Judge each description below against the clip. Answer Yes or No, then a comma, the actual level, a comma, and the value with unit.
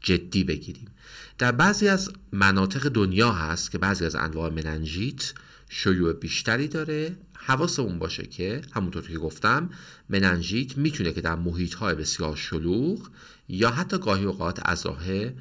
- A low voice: Yes, low, 100 Hz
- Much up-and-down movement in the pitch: Yes, wide, 8.7 semitones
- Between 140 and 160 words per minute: No, average, 130 wpm